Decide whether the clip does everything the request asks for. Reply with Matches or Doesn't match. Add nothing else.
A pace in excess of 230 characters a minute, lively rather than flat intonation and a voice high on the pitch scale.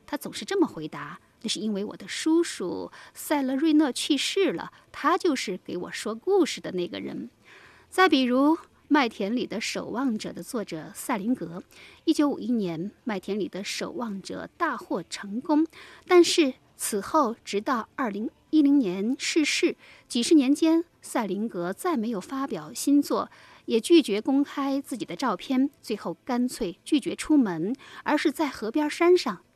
Matches